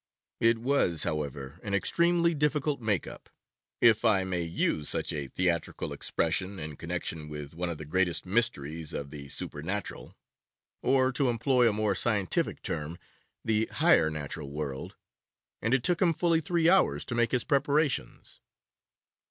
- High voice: No, low, 100 Hz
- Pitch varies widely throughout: Yes, wide, 8.9 semitones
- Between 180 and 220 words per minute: No, average, 150 wpm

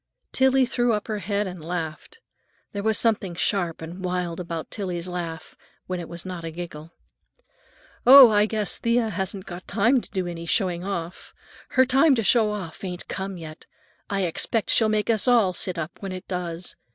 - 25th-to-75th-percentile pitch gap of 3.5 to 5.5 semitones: Yes, average, 4.0 semitones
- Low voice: No, high, 190 Hz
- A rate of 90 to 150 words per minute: No, average, 185 wpm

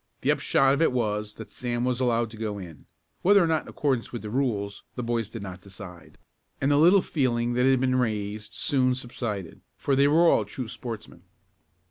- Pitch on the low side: Yes, low, 120 Hz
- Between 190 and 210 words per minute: Yes, fast, 205 wpm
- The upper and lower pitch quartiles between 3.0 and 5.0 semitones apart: Yes, average, 4.0 semitones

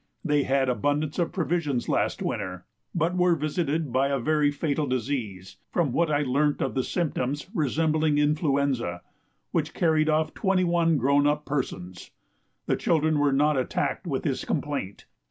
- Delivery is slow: No, average, 155 wpm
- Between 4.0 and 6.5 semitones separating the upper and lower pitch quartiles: No, average, 2.8 semitones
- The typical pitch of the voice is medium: Yes, medium, 145 Hz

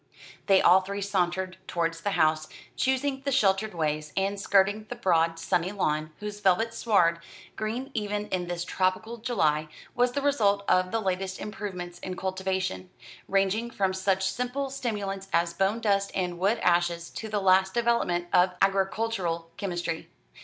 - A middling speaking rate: Yes, average, 155 wpm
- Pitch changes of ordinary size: Yes, average, 3.1 semitones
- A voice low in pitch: No, high, 195 Hz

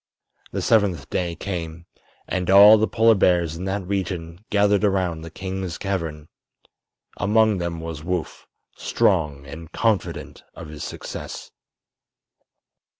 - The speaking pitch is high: No, very low, 90 Hz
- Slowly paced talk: Yes, slow, 125 wpm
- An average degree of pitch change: Yes, average, 3.4 semitones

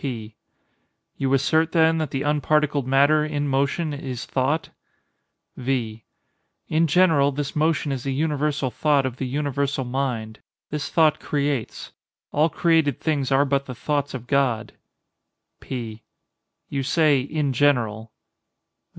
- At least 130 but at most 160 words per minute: Yes, slow, 135 wpm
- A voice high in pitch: No, medium, 140 Hz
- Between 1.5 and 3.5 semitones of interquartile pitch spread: Yes, narrow, 2.6 semitones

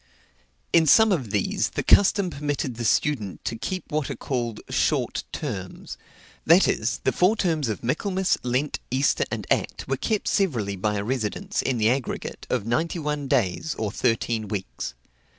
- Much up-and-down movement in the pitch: Yes, wide, 6.5 semitones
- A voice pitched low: Yes, low, 130 Hz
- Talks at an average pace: Yes, average, 170 wpm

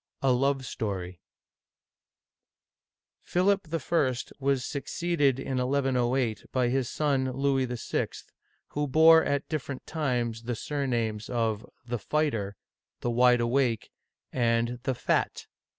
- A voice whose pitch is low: Yes, low, 130 Hz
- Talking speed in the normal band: No, slow, 130 wpm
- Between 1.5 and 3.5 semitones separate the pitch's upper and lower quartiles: Yes, average, 3.0 semitones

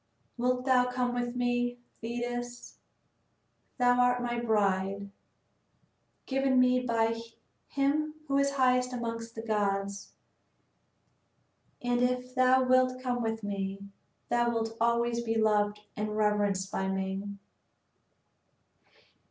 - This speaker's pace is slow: Yes, slow, 110 wpm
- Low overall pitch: No, high, 240 Hz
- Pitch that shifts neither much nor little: Yes, average, 3.1 semitones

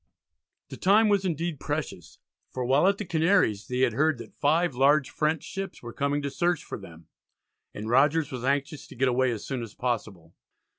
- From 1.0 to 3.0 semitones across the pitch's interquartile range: No, average, 4.9 semitones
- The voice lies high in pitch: No, medium, 140 Hz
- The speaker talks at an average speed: Yes, average, 195 wpm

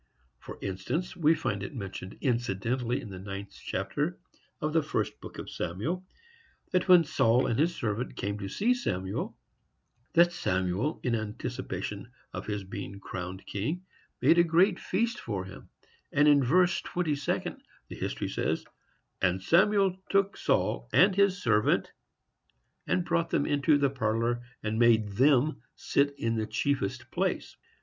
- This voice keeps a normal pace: Yes, average, 155 wpm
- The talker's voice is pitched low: Yes, low, 125 Hz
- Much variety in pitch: Yes, wide, 8.8 semitones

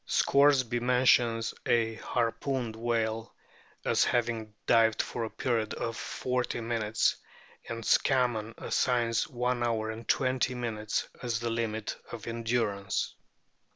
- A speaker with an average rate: No, slow, 120 wpm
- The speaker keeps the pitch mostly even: Yes, narrow, 1.6 semitones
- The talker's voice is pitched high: No, low, 115 Hz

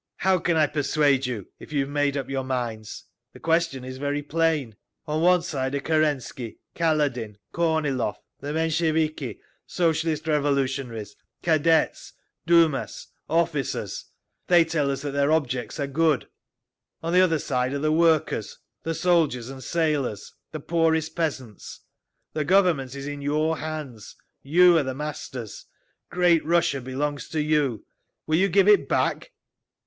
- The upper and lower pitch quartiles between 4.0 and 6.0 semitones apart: No, average, 3.4 semitones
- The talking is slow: No, average, 145 wpm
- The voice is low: No, medium, 150 Hz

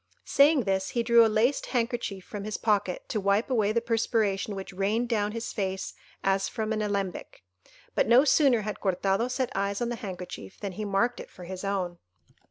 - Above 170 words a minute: Yes, average, 195 wpm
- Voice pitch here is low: No, high, 210 Hz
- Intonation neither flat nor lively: Yes, average, 3.2 semitones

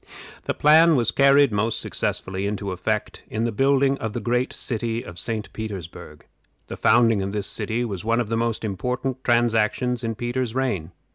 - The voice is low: Yes, low, 115 Hz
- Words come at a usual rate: Yes, average, 180 wpm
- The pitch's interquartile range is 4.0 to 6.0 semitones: No, average, 2.9 semitones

